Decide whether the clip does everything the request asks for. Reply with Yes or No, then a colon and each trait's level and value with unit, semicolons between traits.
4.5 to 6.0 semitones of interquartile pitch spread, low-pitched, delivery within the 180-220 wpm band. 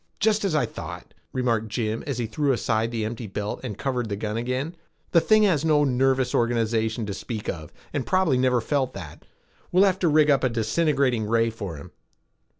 Yes: average, 4.8 semitones; low, 125 Hz; average, 200 wpm